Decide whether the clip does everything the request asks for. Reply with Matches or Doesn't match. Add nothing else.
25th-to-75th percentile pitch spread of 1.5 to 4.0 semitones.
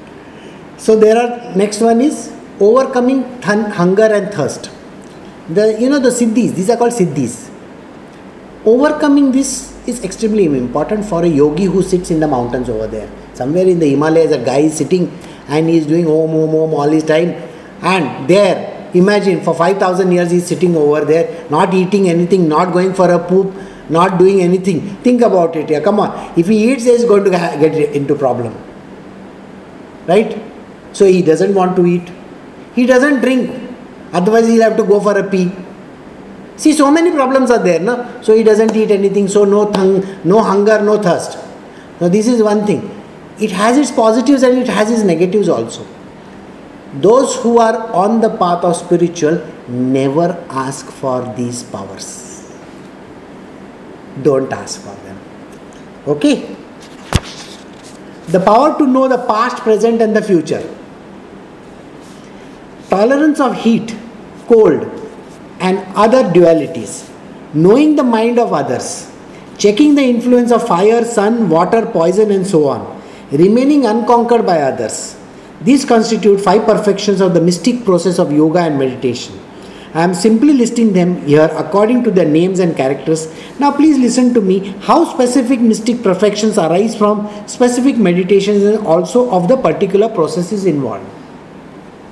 Doesn't match